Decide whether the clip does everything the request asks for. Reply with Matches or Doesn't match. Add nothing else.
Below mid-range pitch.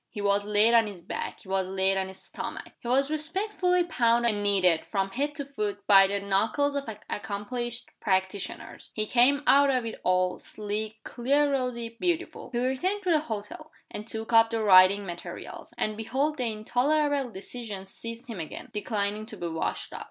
Doesn't match